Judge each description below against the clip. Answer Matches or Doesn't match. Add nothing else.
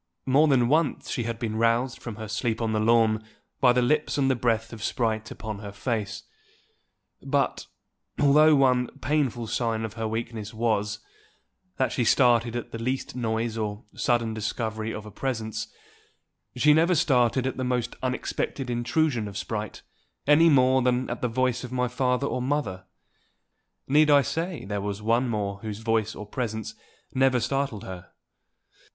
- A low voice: Matches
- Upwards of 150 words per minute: Matches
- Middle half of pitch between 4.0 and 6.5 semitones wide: Doesn't match